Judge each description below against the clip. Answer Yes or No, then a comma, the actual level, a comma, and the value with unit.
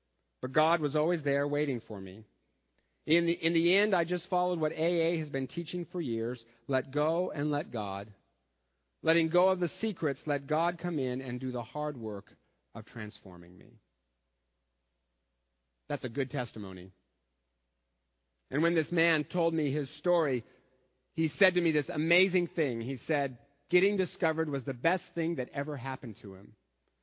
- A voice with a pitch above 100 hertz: Yes, medium, 140 Hz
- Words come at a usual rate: Yes, average, 170 wpm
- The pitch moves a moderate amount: No, wide, 8.9 semitones